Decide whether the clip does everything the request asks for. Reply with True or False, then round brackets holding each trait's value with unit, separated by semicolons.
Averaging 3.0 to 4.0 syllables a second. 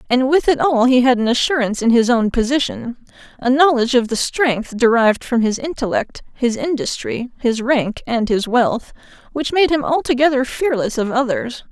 False (5.1 syllables/s)